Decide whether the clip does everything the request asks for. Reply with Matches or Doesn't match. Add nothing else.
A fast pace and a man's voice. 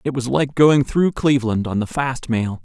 Matches